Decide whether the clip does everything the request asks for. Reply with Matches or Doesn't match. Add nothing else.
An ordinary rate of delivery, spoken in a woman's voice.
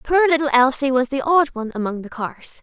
Doesn't match